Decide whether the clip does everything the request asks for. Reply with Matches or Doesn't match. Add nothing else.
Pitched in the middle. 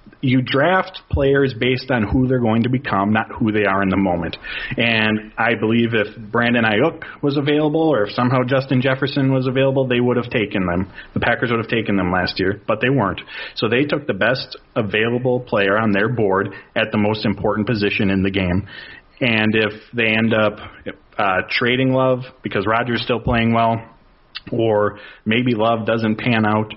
Doesn't match